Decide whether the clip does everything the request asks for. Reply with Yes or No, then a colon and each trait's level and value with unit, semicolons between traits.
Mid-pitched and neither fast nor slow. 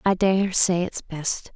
Yes: medium, 180 Hz; average, 195 wpm